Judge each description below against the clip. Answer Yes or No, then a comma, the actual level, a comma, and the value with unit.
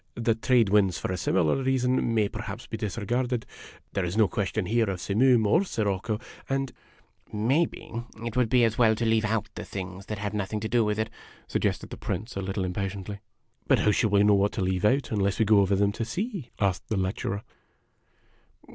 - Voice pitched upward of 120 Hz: No, low, 105 Hz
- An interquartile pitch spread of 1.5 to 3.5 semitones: Yes, average, 3.1 semitones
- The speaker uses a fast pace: Yes, fast, 220 wpm